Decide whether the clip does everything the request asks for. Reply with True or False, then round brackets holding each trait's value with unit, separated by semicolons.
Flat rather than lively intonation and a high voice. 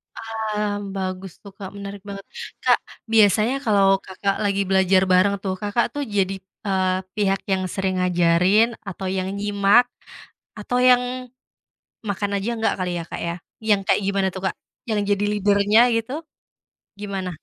True (1.8 semitones; 200 Hz)